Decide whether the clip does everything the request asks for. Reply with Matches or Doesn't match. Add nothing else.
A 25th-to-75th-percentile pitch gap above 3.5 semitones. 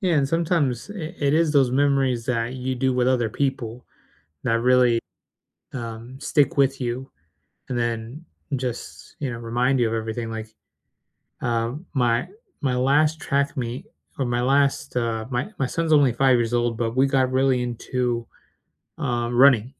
Doesn't match